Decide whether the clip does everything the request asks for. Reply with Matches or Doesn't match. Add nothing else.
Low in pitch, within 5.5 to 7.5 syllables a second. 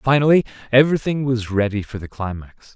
Matches